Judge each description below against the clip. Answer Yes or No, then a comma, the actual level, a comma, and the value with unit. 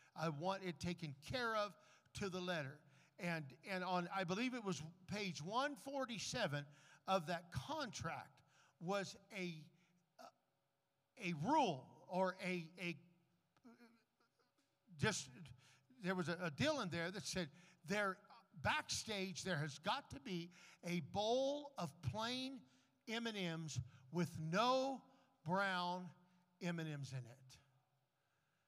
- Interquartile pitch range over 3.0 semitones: Yes, average, 3.8 semitones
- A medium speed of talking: No, slow, 115 wpm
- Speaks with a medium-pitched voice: Yes, medium, 180 Hz